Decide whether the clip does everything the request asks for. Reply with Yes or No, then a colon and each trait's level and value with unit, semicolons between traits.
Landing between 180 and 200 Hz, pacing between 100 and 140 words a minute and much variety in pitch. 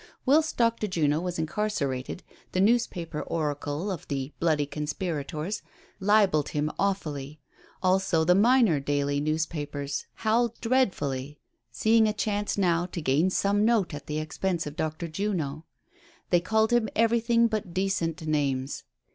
No: medium, 170 Hz; slow, 135 wpm; wide, 5.8 semitones